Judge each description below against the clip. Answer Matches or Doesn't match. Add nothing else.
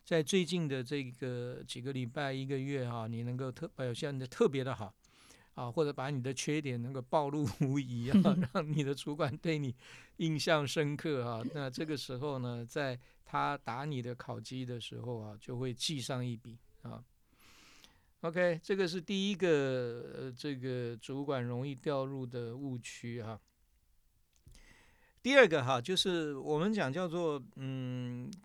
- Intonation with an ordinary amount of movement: Matches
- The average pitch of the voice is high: Doesn't match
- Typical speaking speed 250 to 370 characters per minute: Doesn't match